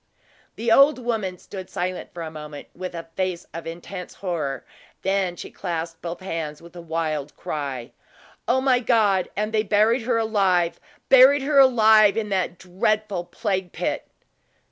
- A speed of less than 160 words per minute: No, average, 165 wpm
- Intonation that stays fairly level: No, average, 4.6 semitones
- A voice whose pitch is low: No, high, 190 Hz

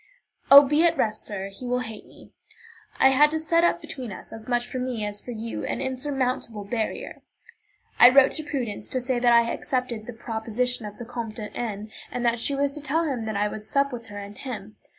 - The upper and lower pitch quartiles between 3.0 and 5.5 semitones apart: Yes, average, 3.6 semitones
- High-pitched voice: Yes, high, 245 Hz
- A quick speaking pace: Yes, fast, 230 wpm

